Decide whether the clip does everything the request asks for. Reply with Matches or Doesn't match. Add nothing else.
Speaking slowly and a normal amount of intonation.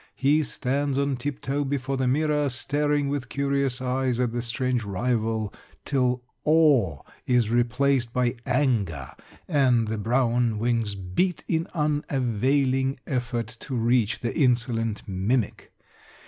Matches